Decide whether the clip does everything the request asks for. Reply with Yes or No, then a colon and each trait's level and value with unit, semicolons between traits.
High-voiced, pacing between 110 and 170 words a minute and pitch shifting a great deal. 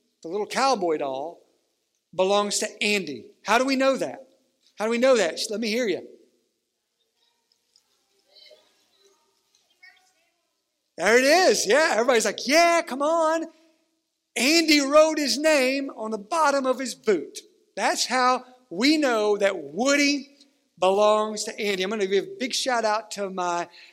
Yes: very high, 265 Hz; average, 150 wpm; wide, 7.2 semitones